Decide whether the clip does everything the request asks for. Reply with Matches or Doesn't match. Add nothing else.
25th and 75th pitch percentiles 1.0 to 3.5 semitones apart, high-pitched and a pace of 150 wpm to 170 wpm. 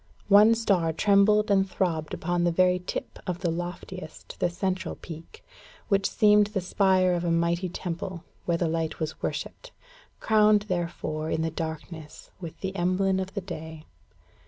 Doesn't match